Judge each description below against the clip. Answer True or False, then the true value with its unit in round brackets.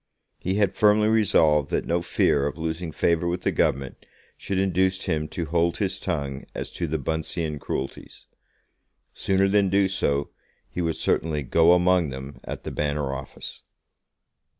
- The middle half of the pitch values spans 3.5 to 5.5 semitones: True (4.1 semitones)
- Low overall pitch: True (85 Hz)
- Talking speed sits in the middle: True (160 wpm)